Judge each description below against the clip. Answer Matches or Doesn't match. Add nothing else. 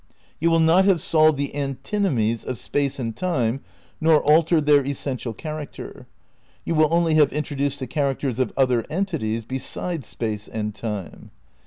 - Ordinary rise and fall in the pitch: Matches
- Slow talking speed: Doesn't match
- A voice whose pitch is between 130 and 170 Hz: Matches